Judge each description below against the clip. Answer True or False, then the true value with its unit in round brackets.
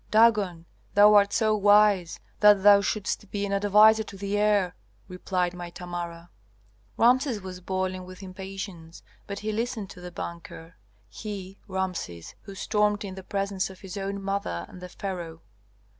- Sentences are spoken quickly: False (160 wpm)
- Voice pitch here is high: True (195 Hz)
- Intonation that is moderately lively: False (2.3 semitones)